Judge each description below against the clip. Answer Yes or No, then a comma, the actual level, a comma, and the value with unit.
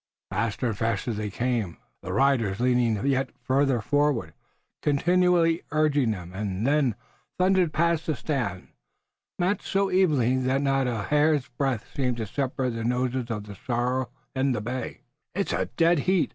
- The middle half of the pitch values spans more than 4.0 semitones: Yes, average, 4.5 semitones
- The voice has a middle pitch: No, low, 130 Hz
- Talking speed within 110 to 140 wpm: No, average, 160 wpm